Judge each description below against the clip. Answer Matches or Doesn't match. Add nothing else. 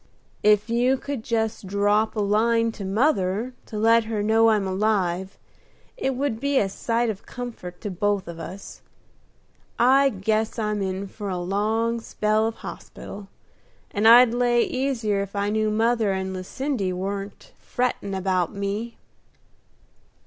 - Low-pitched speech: Doesn't match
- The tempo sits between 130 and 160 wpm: Matches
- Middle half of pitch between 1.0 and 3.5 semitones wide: Matches